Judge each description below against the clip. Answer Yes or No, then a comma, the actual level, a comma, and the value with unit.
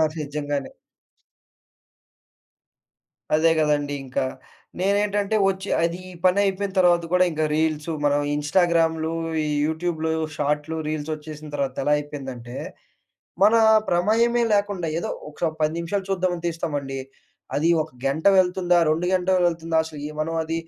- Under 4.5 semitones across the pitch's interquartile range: Yes, average, 3.4 semitones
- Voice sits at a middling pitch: Yes, medium, 160 Hz